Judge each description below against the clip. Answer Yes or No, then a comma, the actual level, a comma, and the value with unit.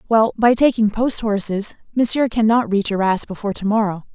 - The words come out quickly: No, average, 175 wpm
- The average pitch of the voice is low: No, high, 215 Hz